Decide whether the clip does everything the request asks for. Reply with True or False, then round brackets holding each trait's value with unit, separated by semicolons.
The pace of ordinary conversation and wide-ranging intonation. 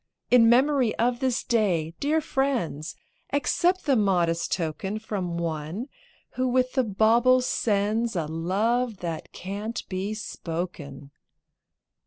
False (120 wpm; 6.4 semitones)